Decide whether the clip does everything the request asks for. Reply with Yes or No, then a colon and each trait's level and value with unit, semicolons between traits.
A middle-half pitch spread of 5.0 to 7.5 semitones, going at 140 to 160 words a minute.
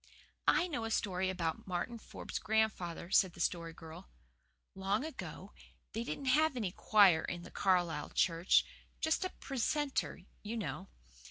Yes: wide, 5.4 semitones; average, 150 wpm